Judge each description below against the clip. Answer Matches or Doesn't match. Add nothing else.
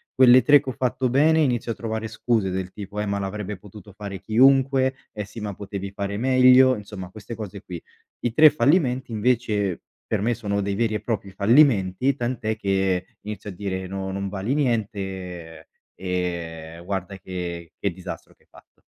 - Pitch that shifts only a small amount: Doesn't match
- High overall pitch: Doesn't match